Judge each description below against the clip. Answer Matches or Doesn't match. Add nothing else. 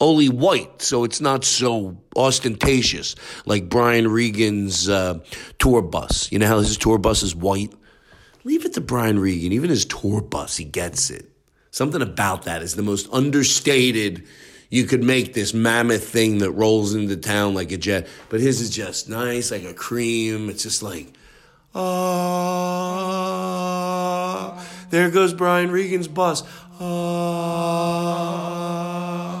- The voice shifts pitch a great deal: Matches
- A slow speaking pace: Doesn't match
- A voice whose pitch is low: Matches